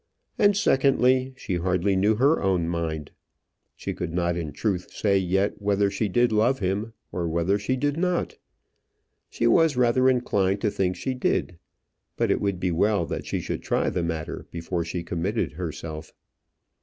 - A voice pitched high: No, very low, 95 Hz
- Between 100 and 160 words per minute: No, average, 170 wpm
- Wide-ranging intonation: Yes, wide, 5.7 semitones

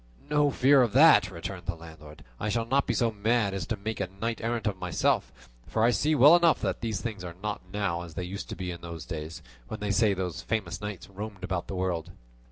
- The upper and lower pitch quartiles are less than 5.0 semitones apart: Yes, average, 4.5 semitones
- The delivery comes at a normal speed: No, fast, 235 wpm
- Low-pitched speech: Yes, low, 100 Hz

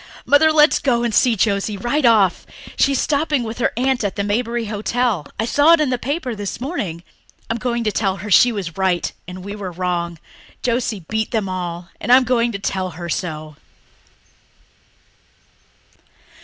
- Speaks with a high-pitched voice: Yes, high, 220 Hz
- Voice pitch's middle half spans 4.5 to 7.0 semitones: Yes, average, 4.9 semitones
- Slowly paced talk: No, average, 180 wpm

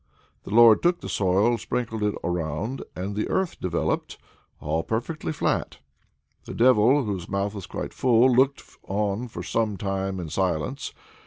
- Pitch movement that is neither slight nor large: Yes, average, 4.1 semitones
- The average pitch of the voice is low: Yes, low, 105 Hz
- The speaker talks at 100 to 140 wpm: No, average, 155 wpm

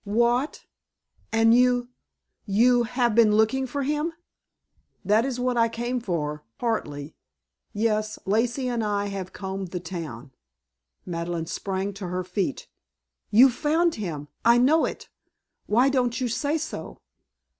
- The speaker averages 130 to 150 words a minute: Yes, slow, 135 wpm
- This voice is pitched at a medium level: No, high, 225 Hz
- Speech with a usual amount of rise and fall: Yes, average, 4.6 semitones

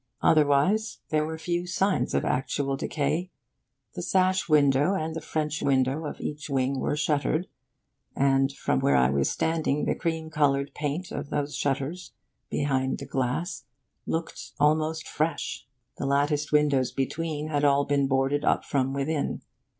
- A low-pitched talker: No, medium, 145 Hz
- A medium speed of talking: Yes, average, 150 wpm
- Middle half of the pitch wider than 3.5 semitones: No, narrow, 2.6 semitones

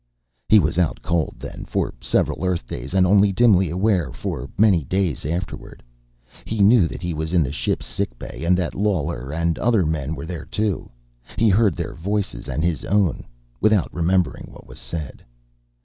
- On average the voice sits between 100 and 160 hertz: No, very low, 85 Hz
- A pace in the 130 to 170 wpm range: No, average, 180 wpm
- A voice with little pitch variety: No, average, 4.2 semitones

